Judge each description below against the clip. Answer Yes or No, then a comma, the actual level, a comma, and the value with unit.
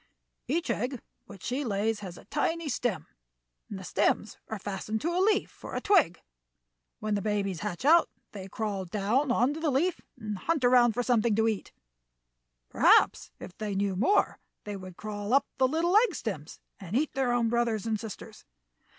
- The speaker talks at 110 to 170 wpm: No, average, 180 wpm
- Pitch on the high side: Yes, high, 220 Hz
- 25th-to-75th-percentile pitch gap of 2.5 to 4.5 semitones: No, average, 5.0 semitones